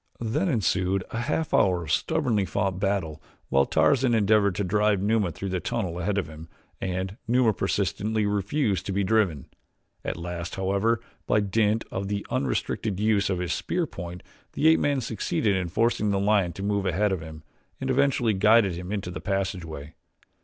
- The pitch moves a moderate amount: Yes, average, 3.2 semitones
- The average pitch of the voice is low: Yes, low, 100 Hz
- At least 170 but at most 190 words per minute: Yes, average, 180 wpm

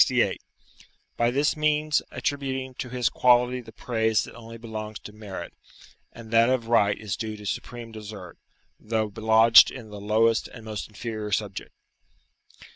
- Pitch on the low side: Yes, low, 115 Hz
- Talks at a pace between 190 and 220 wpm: No, average, 155 wpm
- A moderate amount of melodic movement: No, narrow, 2.3 semitones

